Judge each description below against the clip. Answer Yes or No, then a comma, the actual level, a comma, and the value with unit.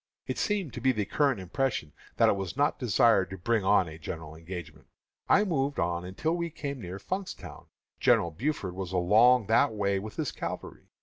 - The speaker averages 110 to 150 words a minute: No, average, 190 wpm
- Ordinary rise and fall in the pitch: No, wide, 7.0 semitones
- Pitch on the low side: Yes, low, 105 Hz